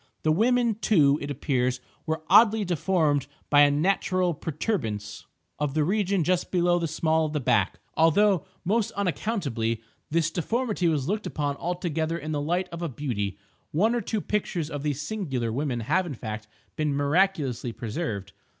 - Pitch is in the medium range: Yes, medium, 160 Hz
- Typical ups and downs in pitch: Yes, average, 4.8 semitones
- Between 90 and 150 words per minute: No, average, 160 wpm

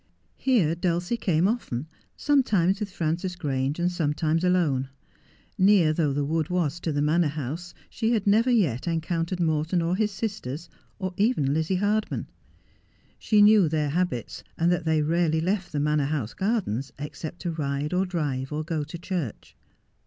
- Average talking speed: Yes, average, 160 wpm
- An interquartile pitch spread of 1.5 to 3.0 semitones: No, average, 3.9 semitones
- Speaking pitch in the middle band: Yes, medium, 165 Hz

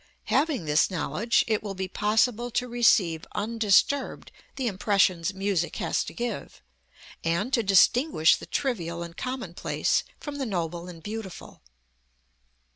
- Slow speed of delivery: Yes, slow, 130 wpm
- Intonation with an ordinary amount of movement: No, wide, 5.7 semitones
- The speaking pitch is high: Yes, high, 205 Hz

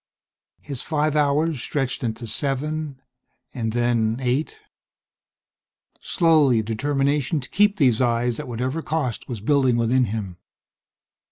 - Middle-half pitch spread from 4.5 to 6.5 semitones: No, average, 4.1 semitones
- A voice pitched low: Yes, low, 130 Hz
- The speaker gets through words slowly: Yes, slow, 120 wpm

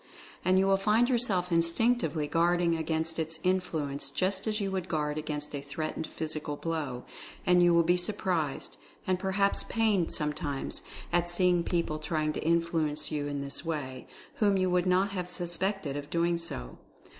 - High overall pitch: No, medium, 170 Hz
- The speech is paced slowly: No, average, 170 wpm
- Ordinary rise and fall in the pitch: Yes, average, 3.4 semitones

